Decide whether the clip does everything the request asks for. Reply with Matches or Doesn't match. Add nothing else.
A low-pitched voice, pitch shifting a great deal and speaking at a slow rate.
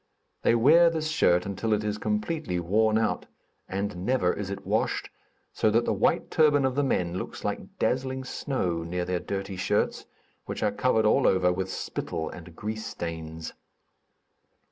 Doesn't match